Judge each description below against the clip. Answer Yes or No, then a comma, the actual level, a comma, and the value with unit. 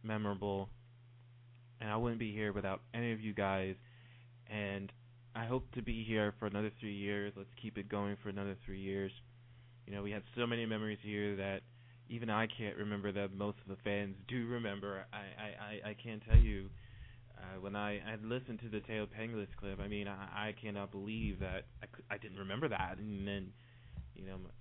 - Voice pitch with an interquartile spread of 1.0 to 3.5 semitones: Yes, average, 2.7 semitones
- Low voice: Yes, low, 105 Hz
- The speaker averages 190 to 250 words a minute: Yes, average, 200 wpm